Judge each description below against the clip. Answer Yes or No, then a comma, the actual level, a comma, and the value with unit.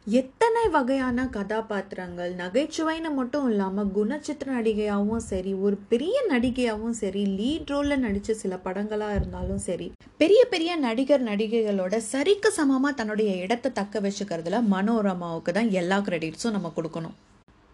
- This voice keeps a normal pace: Yes, average, 120 wpm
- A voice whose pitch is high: Yes, high, 220 Hz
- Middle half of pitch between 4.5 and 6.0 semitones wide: Yes, wide, 5.5 semitones